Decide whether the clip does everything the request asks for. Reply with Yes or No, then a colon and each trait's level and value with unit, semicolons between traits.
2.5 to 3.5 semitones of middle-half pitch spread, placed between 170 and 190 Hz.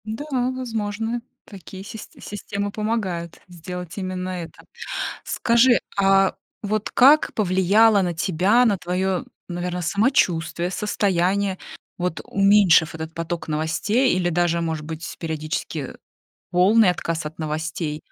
No: average, 3.9 semitones; medium, 185 Hz